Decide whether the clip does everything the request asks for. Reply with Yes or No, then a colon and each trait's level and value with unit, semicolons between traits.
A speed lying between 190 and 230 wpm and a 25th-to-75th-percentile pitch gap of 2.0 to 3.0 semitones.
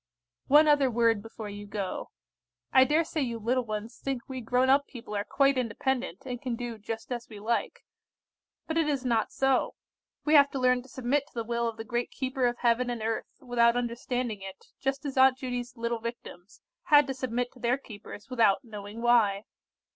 Yes: average, 200 wpm; narrow, 2.6 semitones